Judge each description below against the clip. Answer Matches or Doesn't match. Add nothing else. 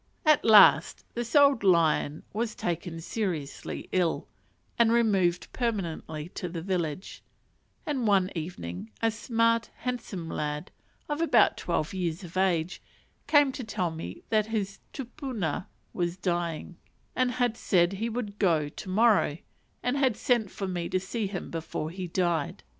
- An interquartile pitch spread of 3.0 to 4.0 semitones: Doesn't match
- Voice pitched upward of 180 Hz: Matches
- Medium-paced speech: Matches